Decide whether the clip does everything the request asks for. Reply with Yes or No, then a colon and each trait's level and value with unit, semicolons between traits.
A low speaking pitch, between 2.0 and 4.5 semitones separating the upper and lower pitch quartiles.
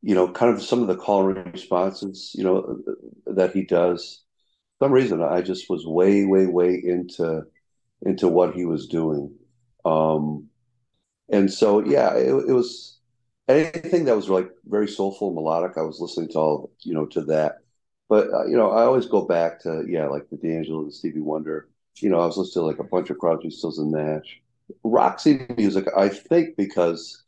Yes: very low, 90 Hz; average, 4.0 semitones